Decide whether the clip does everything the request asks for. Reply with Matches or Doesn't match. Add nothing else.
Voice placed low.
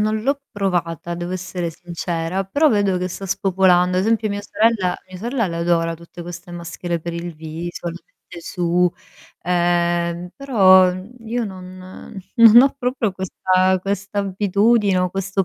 Doesn't match